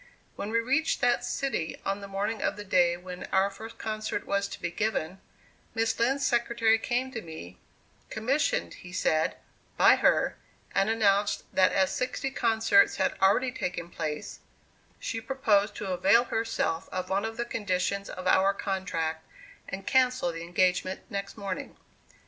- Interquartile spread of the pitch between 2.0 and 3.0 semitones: No, average, 3.8 semitones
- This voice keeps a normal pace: Yes, average, 160 wpm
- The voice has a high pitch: Yes, high, 200 Hz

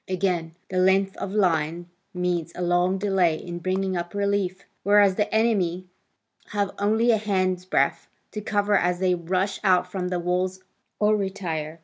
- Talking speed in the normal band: Yes, average, 155 wpm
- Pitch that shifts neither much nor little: No, narrow, 2.2 semitones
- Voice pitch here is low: No, medium, 185 Hz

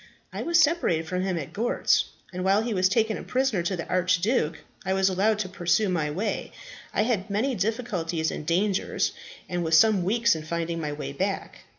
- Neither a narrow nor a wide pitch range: Yes, average, 4.4 semitones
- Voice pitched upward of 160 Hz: Yes, high, 190 Hz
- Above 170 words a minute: Yes, average, 200 wpm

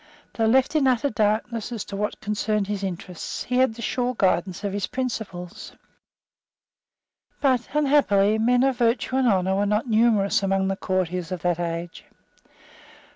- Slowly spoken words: No, average, 160 wpm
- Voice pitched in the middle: No, high, 210 Hz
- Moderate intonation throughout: Yes, average, 4.2 semitones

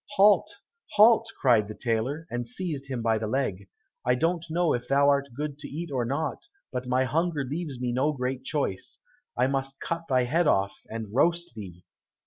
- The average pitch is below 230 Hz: Yes, low, 135 Hz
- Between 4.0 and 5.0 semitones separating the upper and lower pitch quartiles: Yes, average, 4.6 semitones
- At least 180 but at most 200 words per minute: Yes, average, 190 wpm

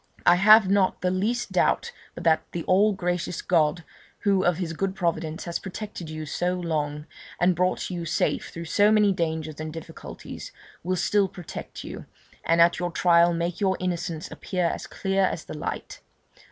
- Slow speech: No, average, 180 wpm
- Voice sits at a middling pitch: Yes, medium, 175 Hz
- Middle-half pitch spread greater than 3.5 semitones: No, narrow, 2.5 semitones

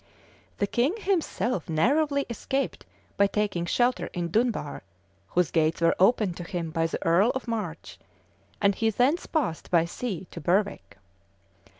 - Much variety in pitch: Yes, wide, 6.6 semitones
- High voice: Yes, high, 200 Hz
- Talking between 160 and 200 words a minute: No, average, 150 wpm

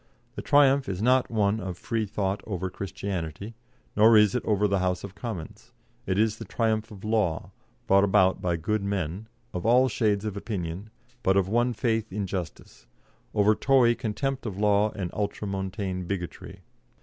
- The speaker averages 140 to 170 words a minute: Yes, average, 165 wpm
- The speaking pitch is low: Yes, low, 100 Hz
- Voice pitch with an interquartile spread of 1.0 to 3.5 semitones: Yes, average, 2.9 semitones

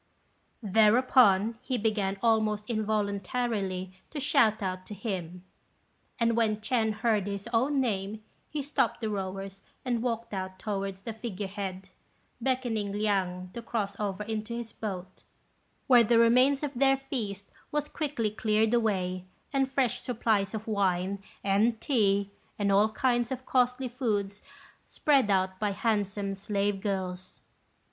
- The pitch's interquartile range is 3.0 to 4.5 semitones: Yes, average, 3.3 semitones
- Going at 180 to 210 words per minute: No, average, 140 wpm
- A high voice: Yes, high, 215 Hz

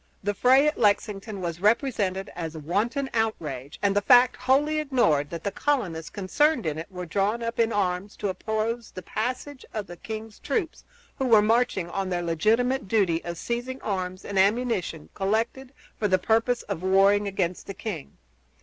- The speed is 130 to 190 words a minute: Yes, average, 175 wpm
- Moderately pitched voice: No, high, 205 Hz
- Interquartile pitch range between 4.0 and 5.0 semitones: Yes, average, 4.6 semitones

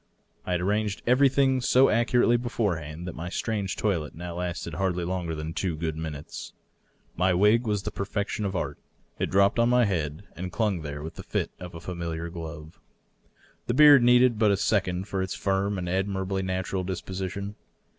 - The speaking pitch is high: No, very low, 95 Hz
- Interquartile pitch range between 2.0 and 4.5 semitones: Yes, average, 3.7 semitones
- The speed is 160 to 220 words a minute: Yes, average, 185 wpm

